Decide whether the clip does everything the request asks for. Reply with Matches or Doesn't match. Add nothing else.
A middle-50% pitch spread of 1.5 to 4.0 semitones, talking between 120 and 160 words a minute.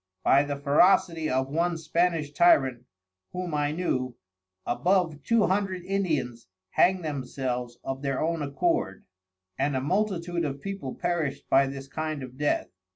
Doesn't match